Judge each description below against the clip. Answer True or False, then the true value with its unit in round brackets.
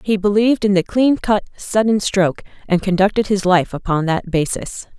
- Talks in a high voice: True (200 Hz)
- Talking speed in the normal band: True (180 wpm)